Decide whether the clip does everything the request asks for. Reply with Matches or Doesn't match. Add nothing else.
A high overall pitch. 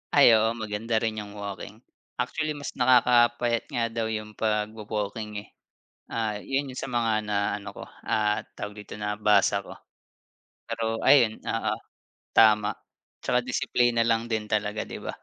Doesn't match